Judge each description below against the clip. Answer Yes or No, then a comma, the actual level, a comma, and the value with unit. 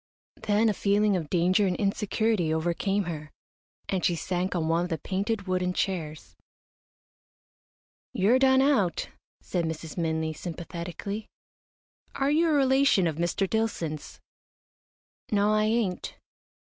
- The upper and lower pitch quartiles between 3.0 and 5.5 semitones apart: Yes, average, 4.0 semitones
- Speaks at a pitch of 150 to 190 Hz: Yes, medium, 185 Hz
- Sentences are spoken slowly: Yes, slow, 130 wpm